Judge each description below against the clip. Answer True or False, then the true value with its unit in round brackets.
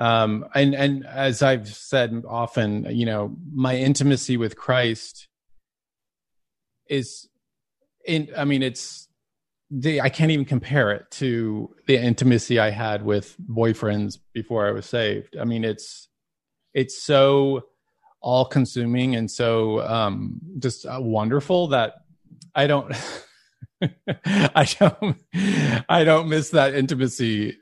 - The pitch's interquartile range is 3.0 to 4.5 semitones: True (3.9 semitones)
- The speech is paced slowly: True (125 wpm)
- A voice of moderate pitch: False (130 Hz)